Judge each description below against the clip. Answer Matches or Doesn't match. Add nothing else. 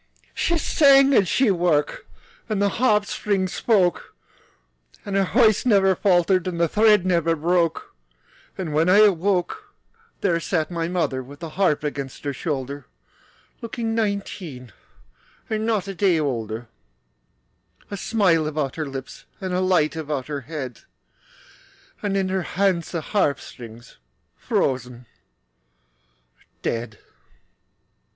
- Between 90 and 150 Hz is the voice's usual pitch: Doesn't match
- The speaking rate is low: Matches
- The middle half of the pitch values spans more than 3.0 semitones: Matches